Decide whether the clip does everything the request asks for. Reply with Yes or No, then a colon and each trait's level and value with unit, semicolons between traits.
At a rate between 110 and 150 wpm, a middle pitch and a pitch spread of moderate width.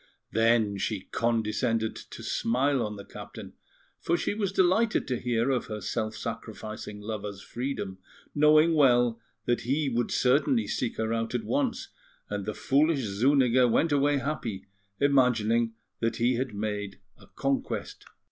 No: average, 145 wpm; low, 120 Hz; average, 4.2 semitones